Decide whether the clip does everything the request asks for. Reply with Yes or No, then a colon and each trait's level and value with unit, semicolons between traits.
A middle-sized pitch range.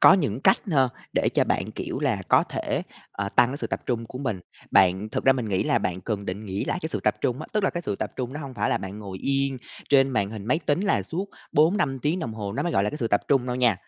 No: wide, 6.0 semitones